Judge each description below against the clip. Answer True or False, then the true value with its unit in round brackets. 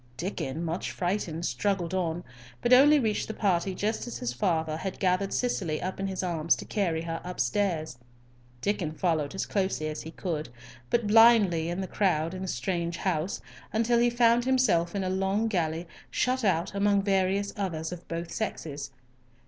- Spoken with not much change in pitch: False (3.8 semitones)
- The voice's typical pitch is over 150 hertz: True (185 Hz)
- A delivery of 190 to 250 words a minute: False (175 wpm)